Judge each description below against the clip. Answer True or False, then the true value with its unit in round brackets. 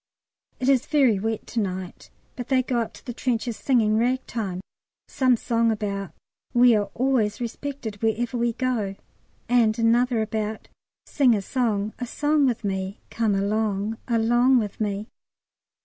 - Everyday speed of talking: True (150 wpm)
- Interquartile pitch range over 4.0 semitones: False (2.8 semitones)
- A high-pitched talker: True (230 Hz)